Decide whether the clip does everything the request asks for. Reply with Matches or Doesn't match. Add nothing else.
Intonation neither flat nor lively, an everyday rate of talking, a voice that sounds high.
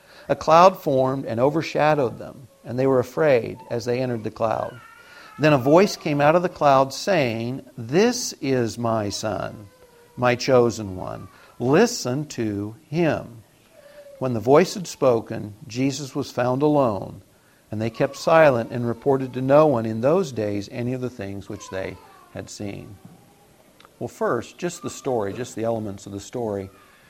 Doesn't match